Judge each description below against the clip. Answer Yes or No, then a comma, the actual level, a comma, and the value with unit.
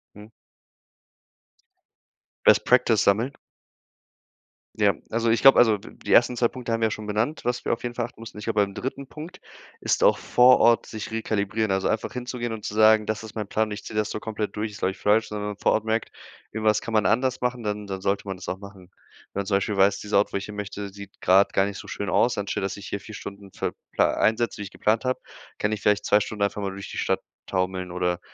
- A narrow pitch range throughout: Yes, narrow, 2.1 semitones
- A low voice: Yes, low, 105 Hz